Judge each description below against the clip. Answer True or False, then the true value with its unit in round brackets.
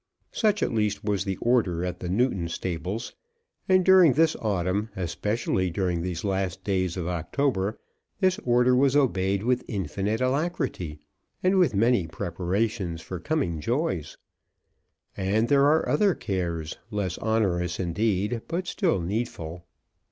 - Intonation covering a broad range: True (6.1 semitones)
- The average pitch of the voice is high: False (100 Hz)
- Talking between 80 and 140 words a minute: True (135 wpm)